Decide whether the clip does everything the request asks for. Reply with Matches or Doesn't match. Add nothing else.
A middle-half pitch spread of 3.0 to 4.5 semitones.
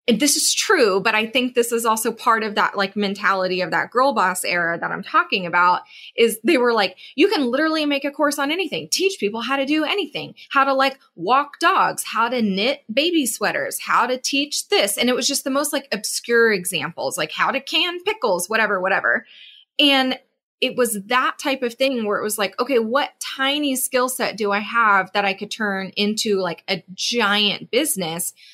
Doesn't match